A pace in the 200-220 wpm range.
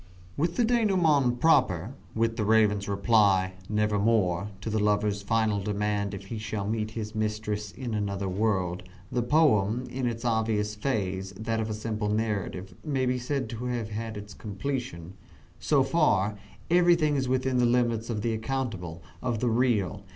No: average, 160 wpm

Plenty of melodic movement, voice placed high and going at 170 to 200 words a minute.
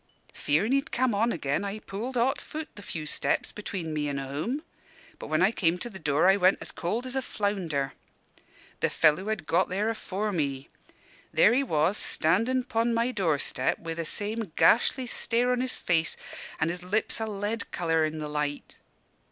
Yes: wide, 6.3 semitones; high, 195 Hz; average, 190 wpm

